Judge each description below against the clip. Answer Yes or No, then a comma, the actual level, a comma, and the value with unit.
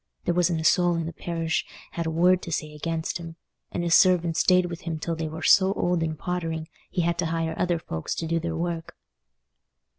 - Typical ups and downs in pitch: No, narrow, 1.4 semitones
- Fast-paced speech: Yes, fast, 220 wpm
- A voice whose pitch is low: No, medium, 165 Hz